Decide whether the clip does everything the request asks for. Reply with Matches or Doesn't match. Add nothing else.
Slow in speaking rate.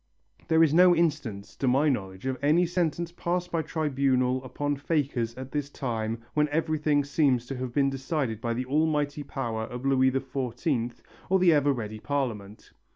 Doesn't match